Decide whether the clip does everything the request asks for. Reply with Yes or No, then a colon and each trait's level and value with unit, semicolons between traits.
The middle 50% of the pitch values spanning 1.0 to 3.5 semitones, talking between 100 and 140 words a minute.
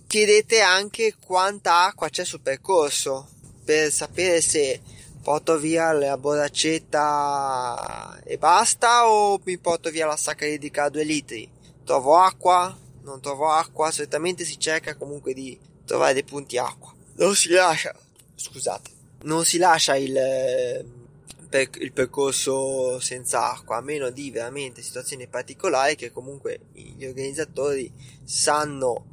No: average, 4.3 semitones; average, 130 wpm